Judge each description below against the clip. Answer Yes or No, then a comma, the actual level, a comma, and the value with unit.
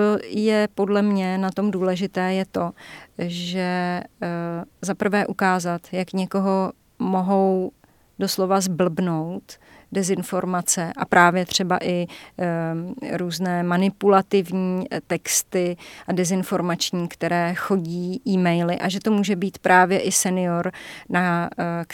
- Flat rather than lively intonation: Yes, narrow, 1.7 semitones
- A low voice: No, medium, 185 Hz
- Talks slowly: Yes, slow, 105 wpm